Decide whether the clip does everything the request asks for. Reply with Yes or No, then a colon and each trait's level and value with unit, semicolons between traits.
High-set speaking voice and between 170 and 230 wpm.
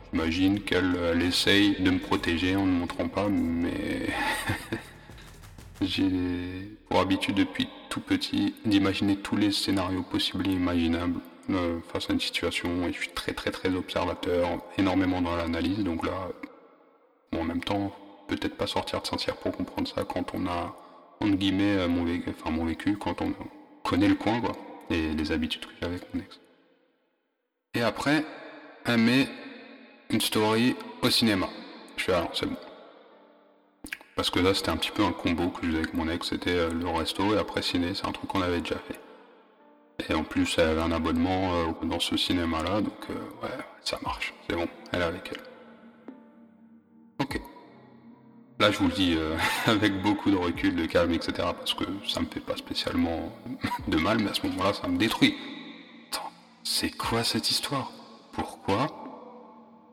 No: low, 125 Hz; average, 180 wpm